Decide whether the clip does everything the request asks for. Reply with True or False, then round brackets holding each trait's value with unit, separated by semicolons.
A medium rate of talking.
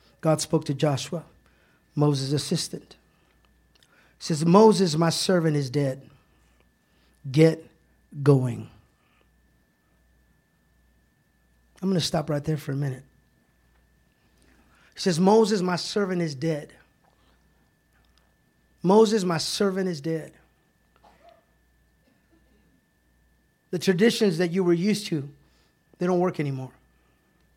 False (100 wpm)